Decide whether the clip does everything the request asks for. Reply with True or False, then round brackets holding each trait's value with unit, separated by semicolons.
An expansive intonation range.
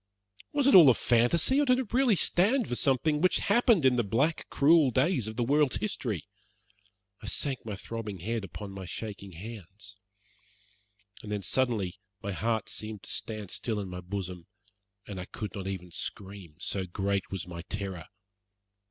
True (6.2 semitones)